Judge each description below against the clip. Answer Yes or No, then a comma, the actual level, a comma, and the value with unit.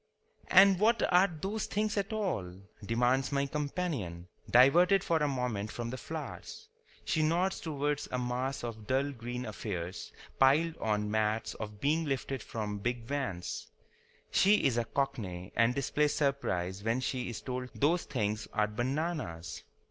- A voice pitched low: Yes, low, 130 Hz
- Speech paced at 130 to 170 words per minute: Yes, average, 150 wpm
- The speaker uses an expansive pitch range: Yes, wide, 5.9 semitones